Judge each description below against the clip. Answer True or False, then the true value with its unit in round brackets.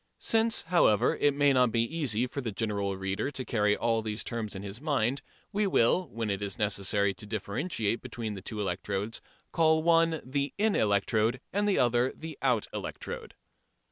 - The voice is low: True (115 Hz)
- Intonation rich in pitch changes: True (5.8 semitones)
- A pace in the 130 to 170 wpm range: False (180 wpm)